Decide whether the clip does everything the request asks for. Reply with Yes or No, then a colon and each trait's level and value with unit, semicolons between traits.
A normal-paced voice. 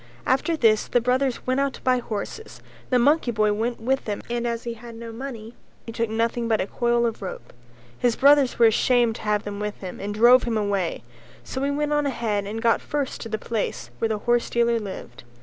No: fast, 225 wpm